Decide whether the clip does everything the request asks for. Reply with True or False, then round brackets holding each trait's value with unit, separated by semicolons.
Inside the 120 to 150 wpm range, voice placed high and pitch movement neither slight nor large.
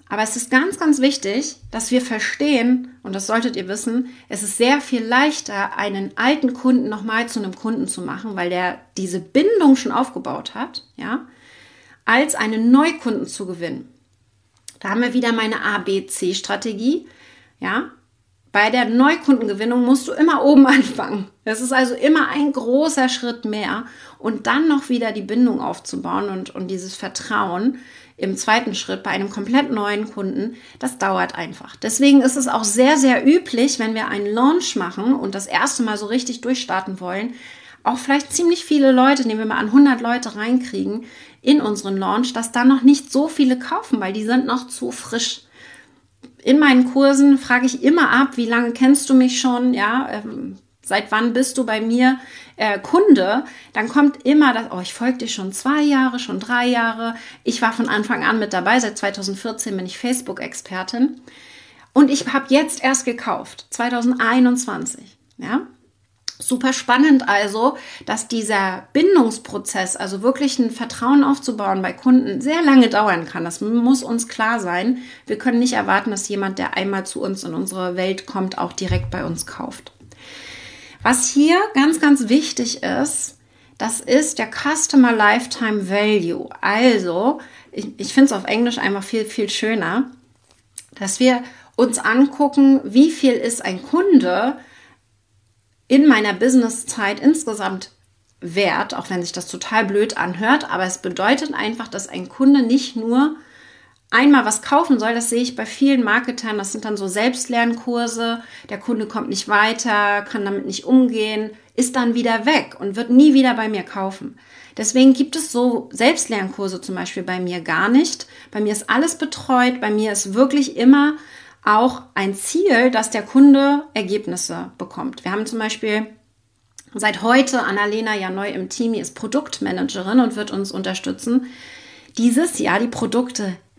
False (165 wpm; 240 Hz; 4.3 semitones)